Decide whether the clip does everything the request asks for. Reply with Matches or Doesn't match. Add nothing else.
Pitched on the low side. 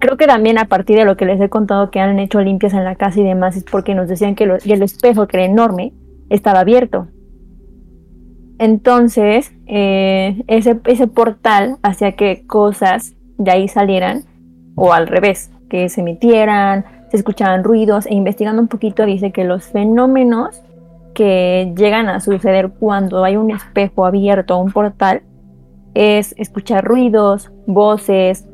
Doesn't match